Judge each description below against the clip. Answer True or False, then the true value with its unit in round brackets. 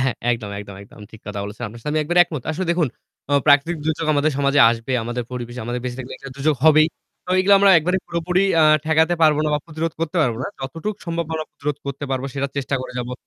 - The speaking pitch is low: False (145 Hz)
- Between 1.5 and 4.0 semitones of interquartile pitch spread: False (4.6 semitones)